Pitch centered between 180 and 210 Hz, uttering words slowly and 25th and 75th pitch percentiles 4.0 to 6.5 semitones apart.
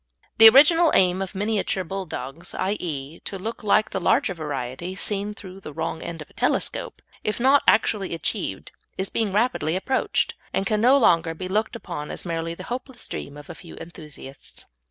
No: high, 190 Hz; average, 180 wpm; average, 4.6 semitones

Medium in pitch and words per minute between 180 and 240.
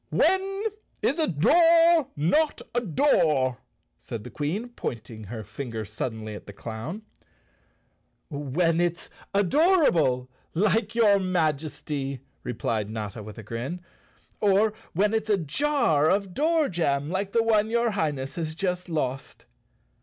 No: medium, 170 Hz; average, 140 wpm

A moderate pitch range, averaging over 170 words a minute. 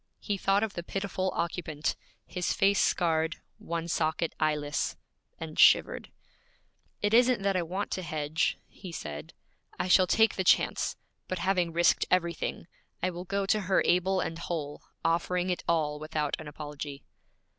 No: average, 3.3 semitones; average, 155 wpm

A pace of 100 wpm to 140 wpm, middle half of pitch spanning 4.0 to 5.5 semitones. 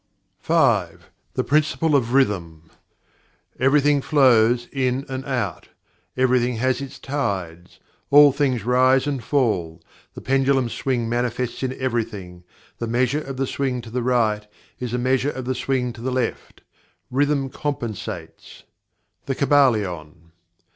No: slow, 135 wpm; average, 3.0 semitones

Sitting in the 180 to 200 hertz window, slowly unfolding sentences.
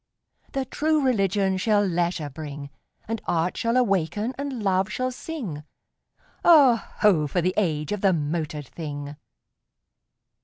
Yes: high, 190 Hz; slow, 130 wpm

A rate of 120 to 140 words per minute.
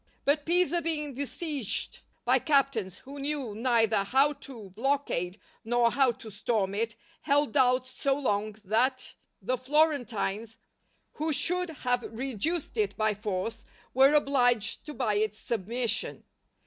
Yes: slow, 135 wpm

